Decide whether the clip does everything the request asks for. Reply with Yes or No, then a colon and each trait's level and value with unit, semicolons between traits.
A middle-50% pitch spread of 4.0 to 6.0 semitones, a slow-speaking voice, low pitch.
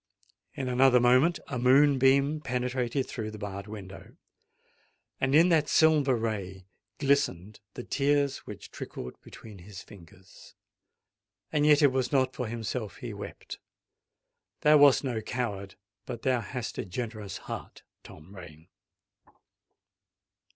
Yes: average, 5.1 semitones; slow, 125 wpm; low, 125 Hz